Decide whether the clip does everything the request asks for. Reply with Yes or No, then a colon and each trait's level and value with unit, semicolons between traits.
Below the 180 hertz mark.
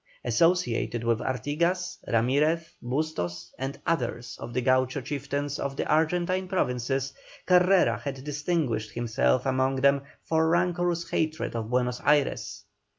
Yes: medium, 140 Hz